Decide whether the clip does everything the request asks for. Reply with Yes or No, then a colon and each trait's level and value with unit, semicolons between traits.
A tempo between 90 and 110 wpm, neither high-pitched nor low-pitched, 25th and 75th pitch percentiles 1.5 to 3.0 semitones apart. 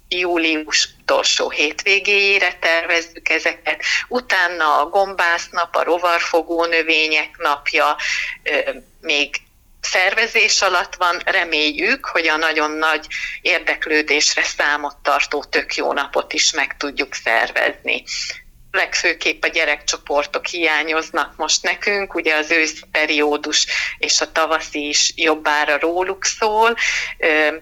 Yes: slow, 105 wpm; medium, 160 Hz; average, 2.7 semitones